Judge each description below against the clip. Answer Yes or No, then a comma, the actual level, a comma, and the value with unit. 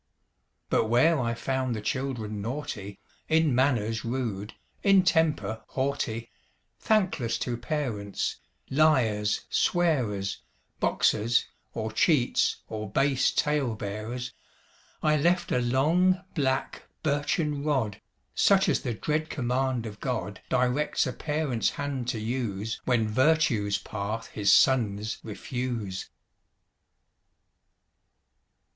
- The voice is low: Yes, low, 125 Hz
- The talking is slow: Yes, slow, 105 wpm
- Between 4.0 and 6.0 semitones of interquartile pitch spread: Yes, average, 5.1 semitones